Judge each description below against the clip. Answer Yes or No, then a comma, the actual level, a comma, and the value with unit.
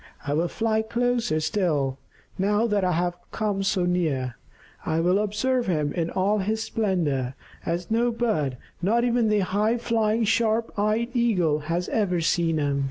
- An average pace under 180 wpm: Yes, average, 165 wpm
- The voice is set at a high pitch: Yes, high, 195 Hz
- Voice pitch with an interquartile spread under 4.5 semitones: No, average, 5.1 semitones